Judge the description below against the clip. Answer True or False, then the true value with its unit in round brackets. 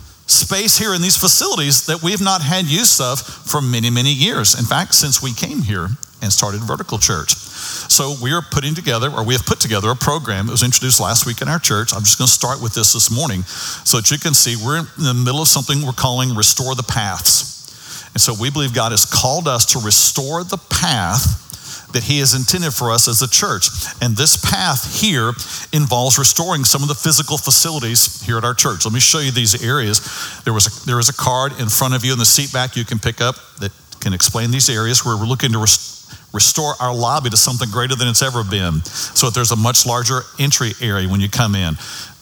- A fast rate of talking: True (235 wpm)